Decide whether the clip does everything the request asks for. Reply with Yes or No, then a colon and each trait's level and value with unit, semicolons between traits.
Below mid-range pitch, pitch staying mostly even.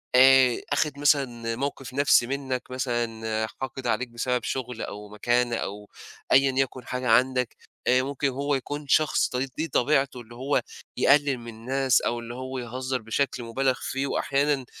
Yes: low, 130 Hz; narrow, 2.3 semitones